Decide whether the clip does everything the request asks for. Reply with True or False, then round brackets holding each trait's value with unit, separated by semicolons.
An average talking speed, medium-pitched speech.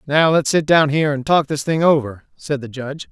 False (250 wpm; 145 Hz)